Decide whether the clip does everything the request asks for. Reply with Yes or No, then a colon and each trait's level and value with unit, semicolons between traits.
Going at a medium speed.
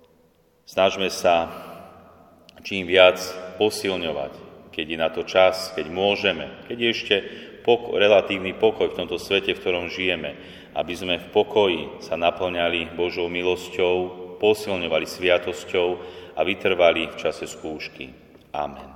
Yes: average, 125 wpm